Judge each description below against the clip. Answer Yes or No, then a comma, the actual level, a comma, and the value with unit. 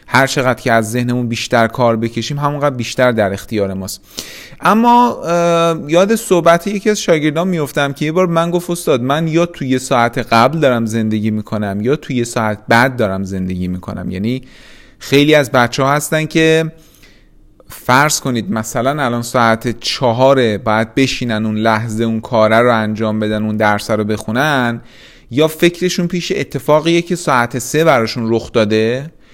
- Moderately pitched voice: No, low, 125 Hz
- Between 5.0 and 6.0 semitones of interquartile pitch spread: Yes, wide, 5.6 semitones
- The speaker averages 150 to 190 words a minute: Yes, fast, 155 wpm